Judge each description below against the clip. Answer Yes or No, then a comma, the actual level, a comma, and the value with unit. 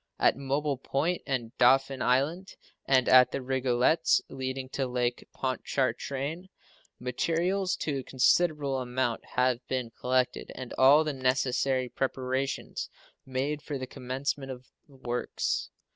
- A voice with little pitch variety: Yes, narrow, 1.7 semitones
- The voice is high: No, low, 130 Hz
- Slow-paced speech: Yes, slow, 130 wpm